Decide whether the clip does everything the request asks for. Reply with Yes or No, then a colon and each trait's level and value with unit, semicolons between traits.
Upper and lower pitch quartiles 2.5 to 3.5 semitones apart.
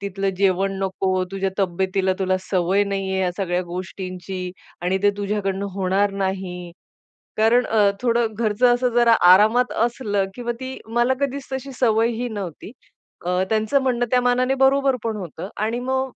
No: average, 4.1 semitones